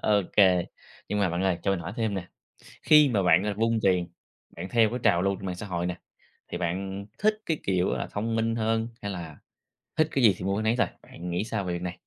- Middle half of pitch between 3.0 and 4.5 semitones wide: Yes, average, 3.9 semitones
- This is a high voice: No, low, 100 Hz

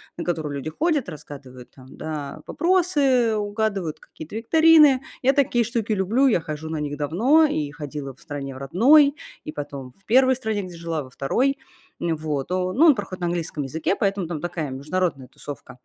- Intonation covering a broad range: Yes, wide, 8.5 semitones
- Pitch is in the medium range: Yes, medium, 175 Hz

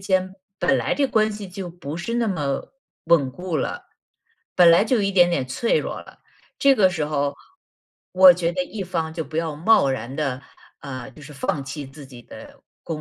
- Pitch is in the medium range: Yes, medium, 170 Hz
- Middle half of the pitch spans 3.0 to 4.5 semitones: No, average, 5.1 semitones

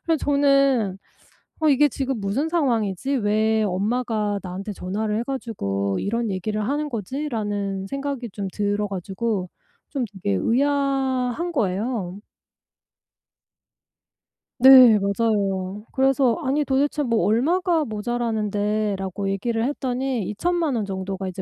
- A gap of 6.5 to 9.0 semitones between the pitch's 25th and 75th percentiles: No, average, 5.2 semitones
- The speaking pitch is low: No, high, 225 Hz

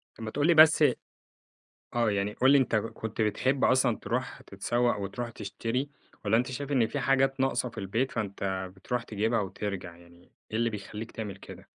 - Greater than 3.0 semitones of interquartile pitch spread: Yes, average, 4.2 semitones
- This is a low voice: Yes, low, 115 Hz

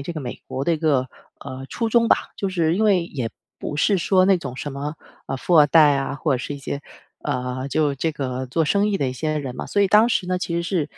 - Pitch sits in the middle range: Yes, medium, 155 Hz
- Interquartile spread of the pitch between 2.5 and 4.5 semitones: No, average, 5.1 semitones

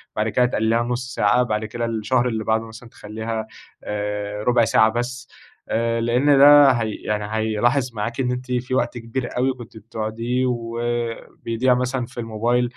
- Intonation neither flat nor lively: No, narrow, 2.0 semitones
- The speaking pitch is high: No, low, 115 Hz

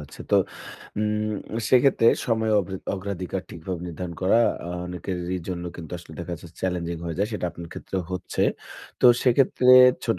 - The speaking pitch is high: No, very low, 90 Hz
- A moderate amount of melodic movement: Yes, average, 3.6 semitones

